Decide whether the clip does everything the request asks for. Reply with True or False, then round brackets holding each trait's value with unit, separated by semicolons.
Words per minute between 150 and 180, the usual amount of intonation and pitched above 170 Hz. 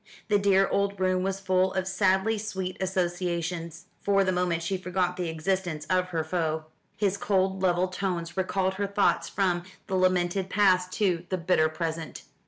False (170 wpm; 1.6 semitones; 185 Hz)